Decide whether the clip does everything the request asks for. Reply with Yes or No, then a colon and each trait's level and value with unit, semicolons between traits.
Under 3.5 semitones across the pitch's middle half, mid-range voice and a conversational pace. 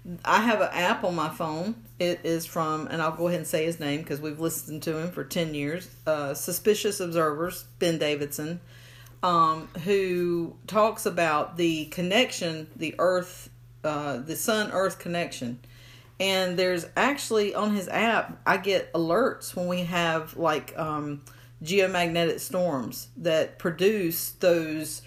Yes: average, 3.1 semitones; medium, 165 Hz; average, 150 wpm